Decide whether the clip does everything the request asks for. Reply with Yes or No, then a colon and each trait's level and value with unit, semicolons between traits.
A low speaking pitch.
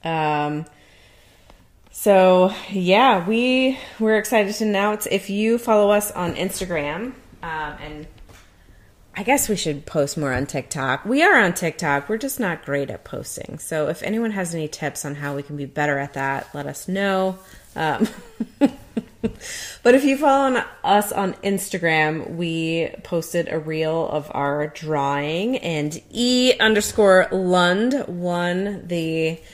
No: medium, 175 Hz